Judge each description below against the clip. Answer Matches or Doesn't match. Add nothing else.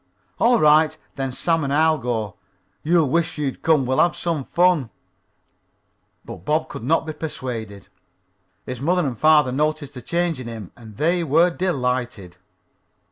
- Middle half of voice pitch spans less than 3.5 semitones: Doesn't match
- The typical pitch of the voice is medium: Matches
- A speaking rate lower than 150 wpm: Doesn't match